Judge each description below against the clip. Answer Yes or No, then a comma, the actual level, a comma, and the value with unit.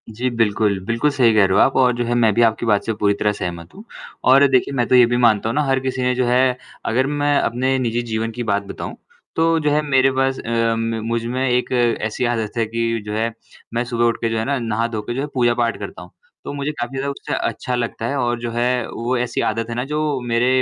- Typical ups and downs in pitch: No, narrow, 2.3 semitones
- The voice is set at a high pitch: No, low, 120 Hz